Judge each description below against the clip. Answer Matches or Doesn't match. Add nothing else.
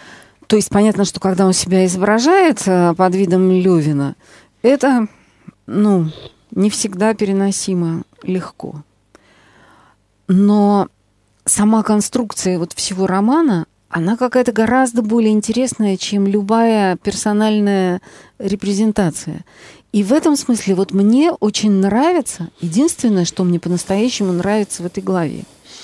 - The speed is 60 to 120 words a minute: Matches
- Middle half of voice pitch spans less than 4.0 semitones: Matches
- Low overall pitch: Doesn't match